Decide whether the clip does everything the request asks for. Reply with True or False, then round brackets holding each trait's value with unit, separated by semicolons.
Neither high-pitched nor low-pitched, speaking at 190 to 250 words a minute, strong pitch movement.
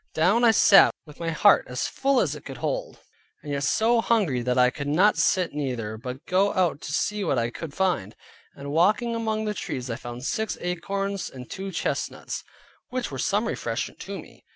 True (180 Hz; 200 wpm; 7.5 semitones)